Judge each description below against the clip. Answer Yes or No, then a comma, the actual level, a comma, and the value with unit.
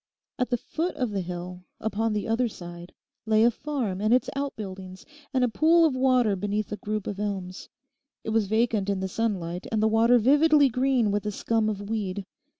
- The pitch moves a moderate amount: Yes, average, 3.9 semitones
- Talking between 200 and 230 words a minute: Yes, fast, 205 wpm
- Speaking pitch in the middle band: No, high, 215 Hz